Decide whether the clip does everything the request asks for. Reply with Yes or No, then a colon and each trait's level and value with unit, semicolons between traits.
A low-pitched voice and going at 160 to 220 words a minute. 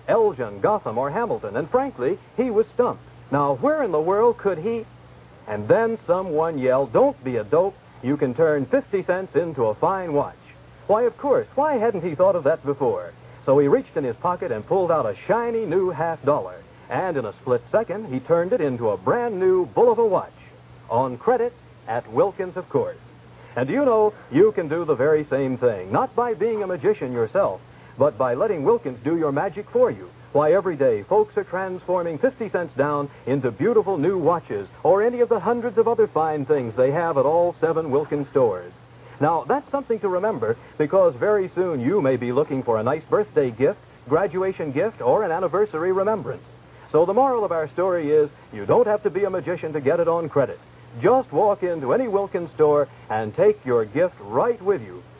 No: high, 205 Hz; fast, 205 wpm